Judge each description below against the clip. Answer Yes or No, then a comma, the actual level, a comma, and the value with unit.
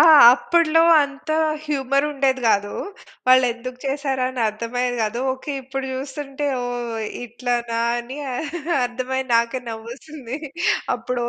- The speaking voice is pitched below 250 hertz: No, very high, 255 Hz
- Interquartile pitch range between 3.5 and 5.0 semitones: No, narrow, 2.5 semitones